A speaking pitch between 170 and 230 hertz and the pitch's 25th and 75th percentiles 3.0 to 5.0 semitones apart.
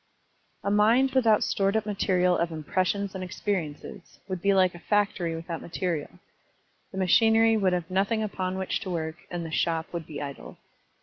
Yes: medium, 185 Hz; average, 3.3 semitones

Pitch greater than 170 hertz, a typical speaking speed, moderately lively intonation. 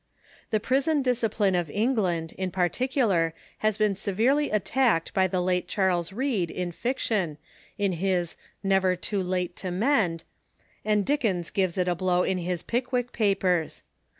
Yes: high, 190 Hz; average, 160 wpm; average, 4.1 semitones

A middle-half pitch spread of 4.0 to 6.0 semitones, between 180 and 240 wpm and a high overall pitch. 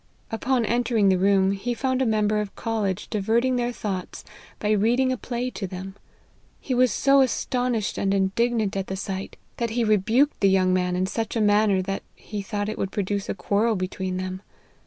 No: average, 3.6 semitones; average, 195 wpm; high, 210 Hz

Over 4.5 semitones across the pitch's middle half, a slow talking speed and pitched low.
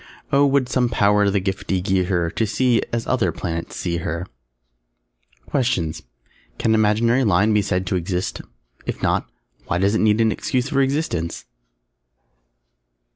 No: average, 5.0 semitones; average, 155 wpm; low, 105 Hz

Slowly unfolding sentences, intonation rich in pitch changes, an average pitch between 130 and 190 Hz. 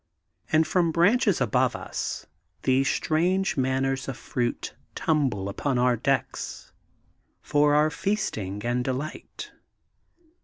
No: slow, 110 wpm; average, 4.1 semitones; low, 135 Hz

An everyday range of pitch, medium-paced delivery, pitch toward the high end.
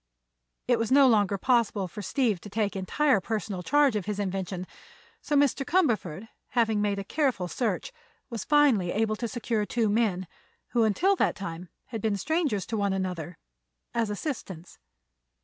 Yes: average, 4.2 semitones; average, 165 wpm; high, 215 Hz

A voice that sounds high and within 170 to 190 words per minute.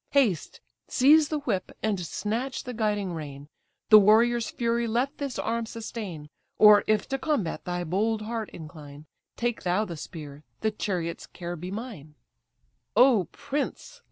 No: high, 215 Hz; average, 150 wpm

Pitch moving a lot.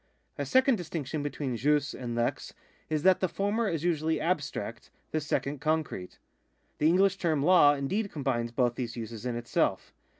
Yes: wide, 5.7 semitones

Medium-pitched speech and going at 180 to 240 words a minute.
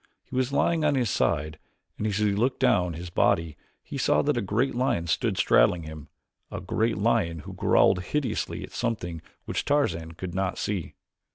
No: low, 100 Hz; average, 185 wpm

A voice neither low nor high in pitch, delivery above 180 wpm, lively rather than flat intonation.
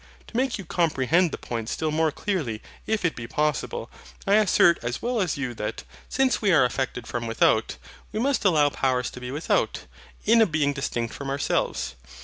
Yes: medium, 150 Hz; average, 190 wpm; wide, 7.5 semitones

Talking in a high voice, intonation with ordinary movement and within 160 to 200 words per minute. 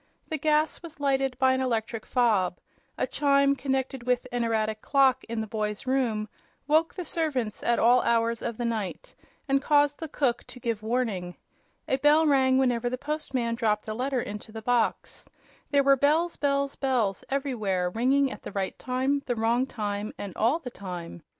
Yes: very high, 250 Hz; average, 4.0 semitones; average, 180 wpm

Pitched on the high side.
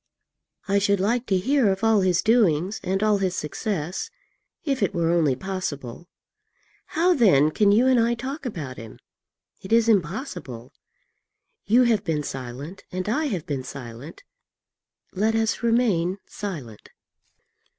Yes: high, 195 Hz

